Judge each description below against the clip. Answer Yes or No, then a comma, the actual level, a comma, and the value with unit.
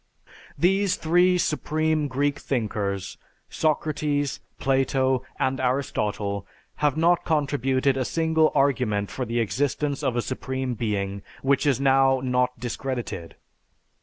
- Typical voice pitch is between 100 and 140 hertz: Yes, low, 135 Hz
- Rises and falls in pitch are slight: No, average, 3.2 semitones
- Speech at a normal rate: No, slow, 115 wpm